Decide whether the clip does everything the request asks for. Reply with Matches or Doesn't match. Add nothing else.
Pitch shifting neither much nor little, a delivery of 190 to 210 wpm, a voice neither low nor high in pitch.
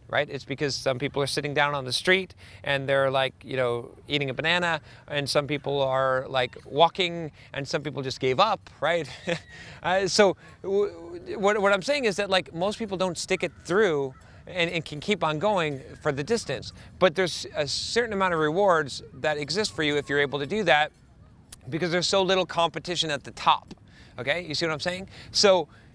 Matches